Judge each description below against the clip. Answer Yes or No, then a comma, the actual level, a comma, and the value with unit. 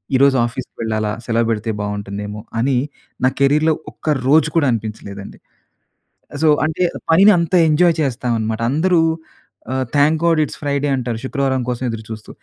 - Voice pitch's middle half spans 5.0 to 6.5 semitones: Yes, wide, 5.4 semitones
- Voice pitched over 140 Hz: No, low, 130 Hz